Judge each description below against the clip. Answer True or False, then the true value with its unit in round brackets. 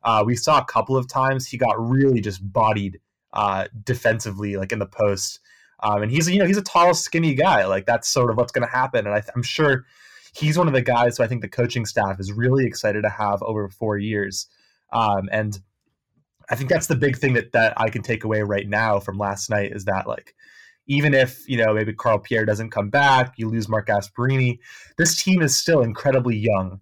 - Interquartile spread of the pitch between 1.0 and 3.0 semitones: False (4.3 semitones)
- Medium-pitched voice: False (115 Hz)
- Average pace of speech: False (225 wpm)